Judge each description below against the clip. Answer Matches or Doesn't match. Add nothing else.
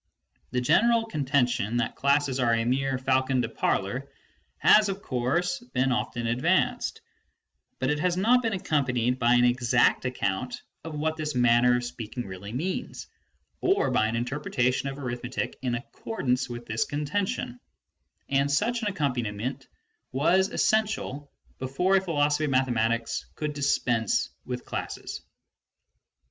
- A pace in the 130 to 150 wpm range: Matches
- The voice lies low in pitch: Matches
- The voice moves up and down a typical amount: Matches